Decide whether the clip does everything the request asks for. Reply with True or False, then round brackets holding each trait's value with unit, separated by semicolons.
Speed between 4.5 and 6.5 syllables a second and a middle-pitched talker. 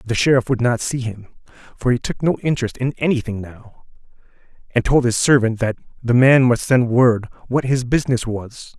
False (5.3 syllables/s; 120 Hz)